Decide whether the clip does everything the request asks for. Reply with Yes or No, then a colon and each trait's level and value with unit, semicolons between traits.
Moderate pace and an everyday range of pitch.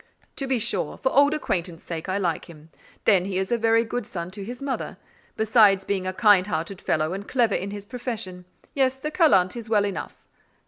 No: fast, 210 wpm; average, 4.5 semitones